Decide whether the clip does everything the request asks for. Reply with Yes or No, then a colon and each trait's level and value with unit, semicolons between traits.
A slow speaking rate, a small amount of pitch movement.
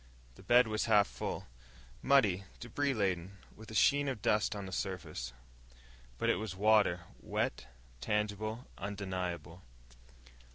No: slow, 130 wpm; average, 3.0 semitones